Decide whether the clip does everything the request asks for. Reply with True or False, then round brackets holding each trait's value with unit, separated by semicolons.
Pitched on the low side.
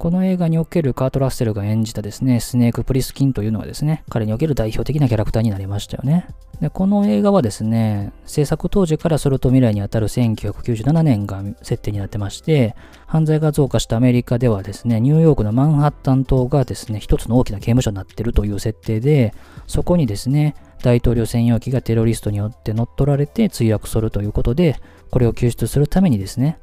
True (125 Hz)